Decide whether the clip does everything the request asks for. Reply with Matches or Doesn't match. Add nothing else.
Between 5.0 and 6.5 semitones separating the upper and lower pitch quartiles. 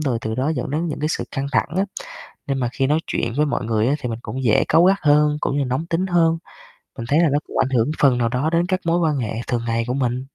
Doesn't match